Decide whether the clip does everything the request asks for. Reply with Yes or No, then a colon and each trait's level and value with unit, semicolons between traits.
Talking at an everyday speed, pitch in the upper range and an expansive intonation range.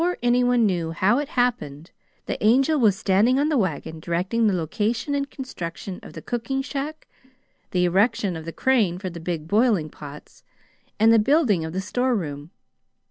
Yes: average, 180 wpm; high, 210 Hz; wide, 6.6 semitones